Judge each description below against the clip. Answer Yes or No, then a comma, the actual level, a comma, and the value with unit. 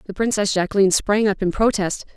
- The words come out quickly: No, average, 195 wpm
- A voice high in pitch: Yes, high, 200 Hz